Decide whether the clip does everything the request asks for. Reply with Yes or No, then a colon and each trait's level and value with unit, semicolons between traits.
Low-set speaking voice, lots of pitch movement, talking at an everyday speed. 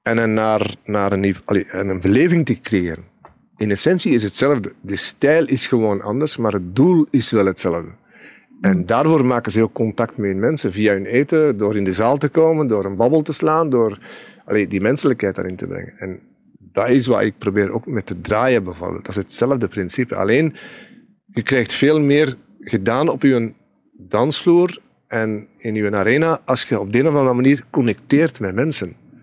Yes: low, 115 Hz; wide, 6.4 semitones; average, 190 wpm